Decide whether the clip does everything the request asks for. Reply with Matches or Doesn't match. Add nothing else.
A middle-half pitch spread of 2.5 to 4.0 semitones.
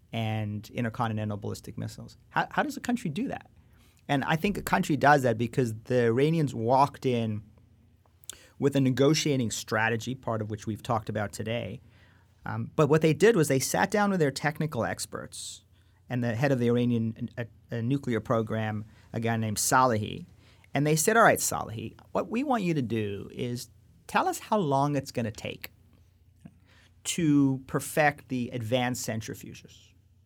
Doesn't match